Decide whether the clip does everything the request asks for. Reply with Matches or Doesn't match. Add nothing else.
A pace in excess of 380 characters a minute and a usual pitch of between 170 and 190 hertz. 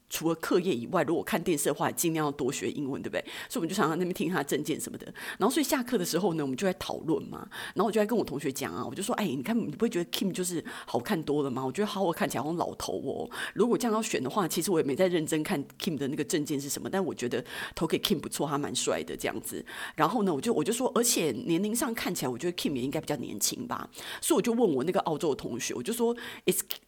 Matches